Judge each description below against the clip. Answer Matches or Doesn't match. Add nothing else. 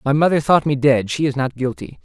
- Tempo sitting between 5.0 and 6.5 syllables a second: Matches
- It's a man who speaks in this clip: Matches